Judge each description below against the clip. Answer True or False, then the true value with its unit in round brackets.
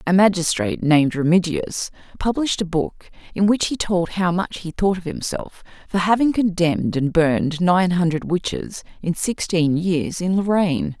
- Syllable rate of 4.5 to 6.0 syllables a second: True (4.8 syllables/s)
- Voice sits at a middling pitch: True (180 Hz)